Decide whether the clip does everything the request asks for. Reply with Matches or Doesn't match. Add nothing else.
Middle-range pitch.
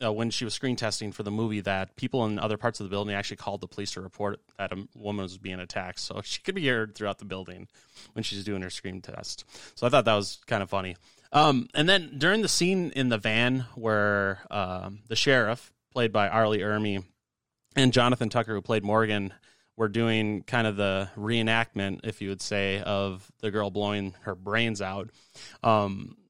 Doesn't match